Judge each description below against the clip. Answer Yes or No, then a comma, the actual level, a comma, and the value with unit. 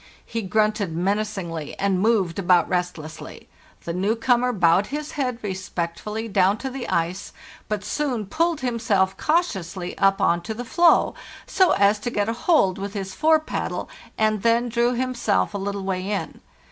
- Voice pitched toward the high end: Yes, high, 205 Hz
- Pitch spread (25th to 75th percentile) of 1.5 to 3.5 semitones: No, average, 4.2 semitones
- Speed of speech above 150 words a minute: Yes, average, 170 wpm